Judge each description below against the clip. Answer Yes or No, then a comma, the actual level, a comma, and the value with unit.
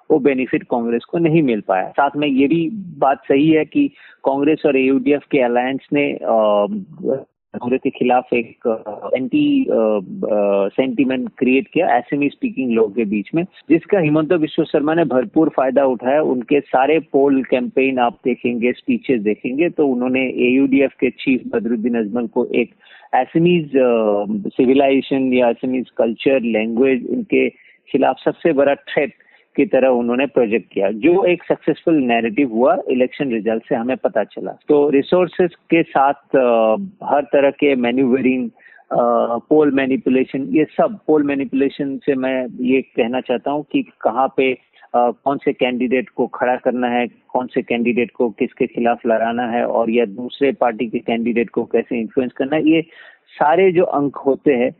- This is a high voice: No, low, 135 Hz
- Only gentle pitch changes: No, average, 3.7 semitones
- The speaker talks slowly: No, average, 160 wpm